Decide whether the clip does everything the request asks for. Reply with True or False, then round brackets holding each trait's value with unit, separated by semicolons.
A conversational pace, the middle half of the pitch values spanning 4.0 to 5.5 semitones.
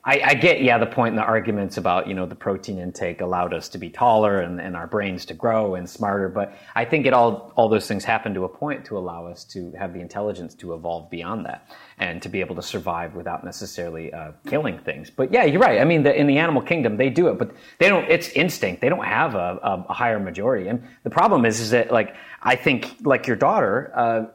False (250 wpm; 4.3 semitones)